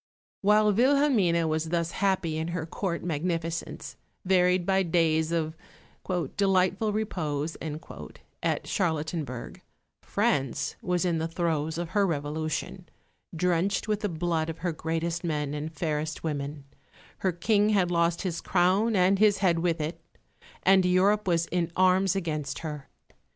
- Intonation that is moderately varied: Yes, average, 3.0 semitones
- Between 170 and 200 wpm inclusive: No, average, 140 wpm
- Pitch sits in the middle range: Yes, medium, 170 Hz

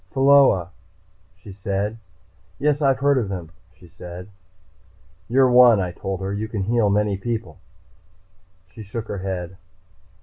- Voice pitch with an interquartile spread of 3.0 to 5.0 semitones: Yes, average, 4.2 semitones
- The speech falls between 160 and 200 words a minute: No, average, 140 wpm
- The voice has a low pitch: Yes, low, 105 Hz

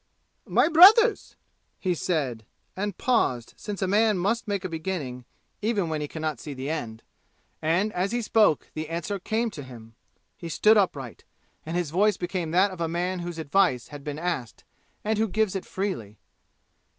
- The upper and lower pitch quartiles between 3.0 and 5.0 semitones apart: No, wide, 5.4 semitones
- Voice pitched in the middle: Yes, medium, 175 Hz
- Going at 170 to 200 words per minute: Yes, average, 180 wpm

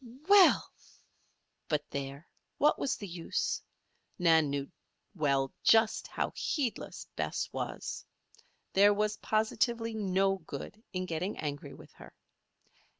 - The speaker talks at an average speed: No, slow, 115 wpm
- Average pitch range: No, wide, 6.0 semitones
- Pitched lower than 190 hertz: No, high, 195 Hz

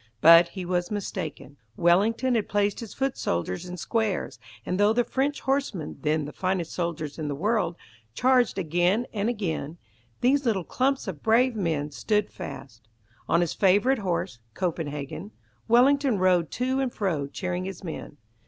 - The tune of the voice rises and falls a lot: Yes, wide, 5.7 semitones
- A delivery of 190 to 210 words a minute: No, average, 160 wpm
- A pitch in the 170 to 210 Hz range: Yes, high, 190 Hz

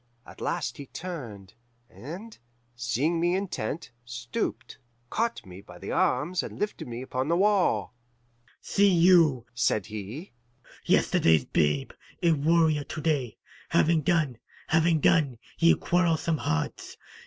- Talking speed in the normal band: No, slow, 130 wpm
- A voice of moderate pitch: Yes, medium, 150 Hz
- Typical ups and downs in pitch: No, wide, 6.4 semitones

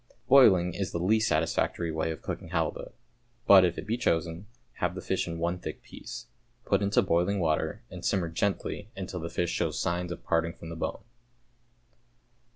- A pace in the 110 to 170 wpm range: No, average, 180 wpm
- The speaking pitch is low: Yes, very low, 85 Hz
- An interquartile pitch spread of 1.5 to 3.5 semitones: Yes, average, 2.9 semitones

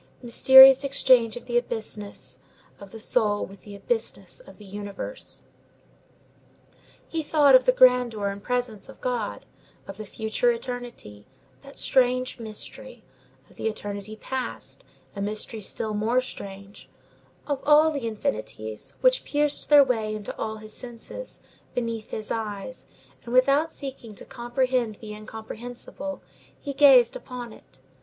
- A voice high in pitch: Yes, high, 235 Hz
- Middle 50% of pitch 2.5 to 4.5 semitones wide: Yes, average, 3.7 semitones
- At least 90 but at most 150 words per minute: Yes, average, 140 wpm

